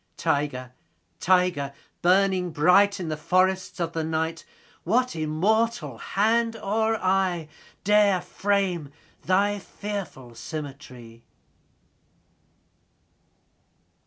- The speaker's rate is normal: No, slow, 90 wpm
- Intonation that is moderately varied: Yes, average, 4.6 semitones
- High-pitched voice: No, medium, 180 Hz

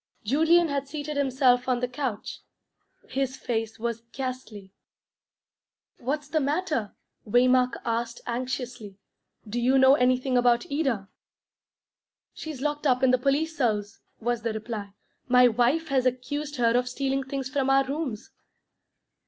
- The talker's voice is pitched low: No, very high, 255 Hz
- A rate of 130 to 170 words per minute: Yes, slow, 135 wpm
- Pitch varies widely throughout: No, average, 2.7 semitones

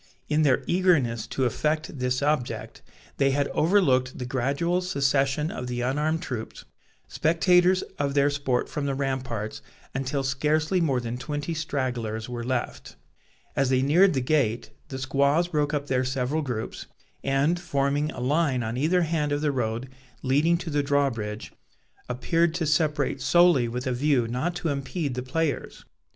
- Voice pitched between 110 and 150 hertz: Yes, medium, 140 Hz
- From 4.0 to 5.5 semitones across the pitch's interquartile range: No, average, 3.5 semitones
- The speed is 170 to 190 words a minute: No, average, 160 wpm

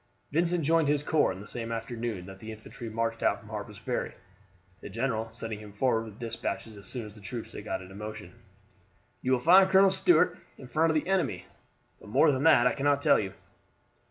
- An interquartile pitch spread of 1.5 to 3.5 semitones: No, wide, 5.4 semitones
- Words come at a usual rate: No, fast, 215 wpm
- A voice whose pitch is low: Yes, low, 115 Hz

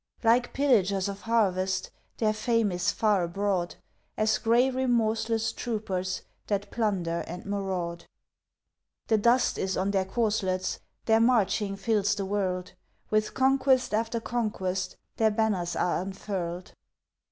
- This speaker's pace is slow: Yes, slow, 125 wpm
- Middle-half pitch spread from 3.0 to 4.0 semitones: Yes, average, 3.3 semitones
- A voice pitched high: Yes, high, 205 Hz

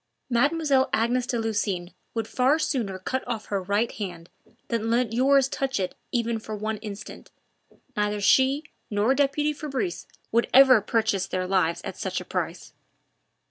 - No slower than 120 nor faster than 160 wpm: Yes, average, 155 wpm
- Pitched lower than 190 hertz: No, high, 225 Hz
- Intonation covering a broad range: No, average, 4.3 semitones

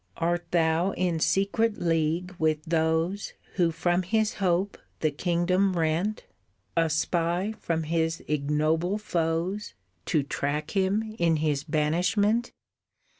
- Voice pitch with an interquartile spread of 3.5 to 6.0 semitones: No, average, 2.9 semitones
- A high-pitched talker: No, medium, 170 Hz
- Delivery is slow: Yes, slow, 120 wpm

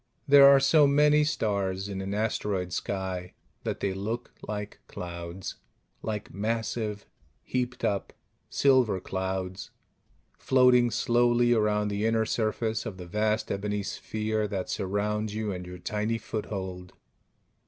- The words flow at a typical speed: No, slow, 130 wpm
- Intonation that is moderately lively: Yes, average, 3.0 semitones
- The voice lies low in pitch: Yes, low, 105 Hz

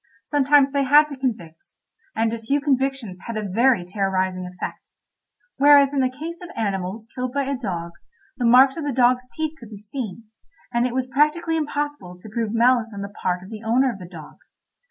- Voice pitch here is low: No, high, 245 Hz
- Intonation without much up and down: No, wide, 5.5 semitones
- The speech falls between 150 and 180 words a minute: No, average, 195 wpm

